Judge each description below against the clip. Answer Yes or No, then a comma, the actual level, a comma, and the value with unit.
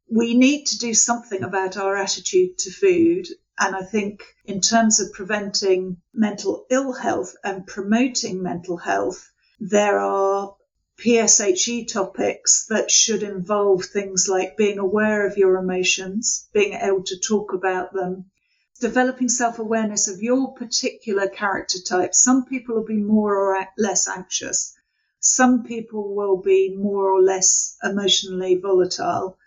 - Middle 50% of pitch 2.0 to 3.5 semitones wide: Yes, average, 3.2 semitones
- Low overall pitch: No, high, 200 Hz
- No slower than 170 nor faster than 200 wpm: No, average, 140 wpm